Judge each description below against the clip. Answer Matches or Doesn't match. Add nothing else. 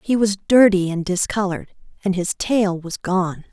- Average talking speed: Matches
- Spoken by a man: Doesn't match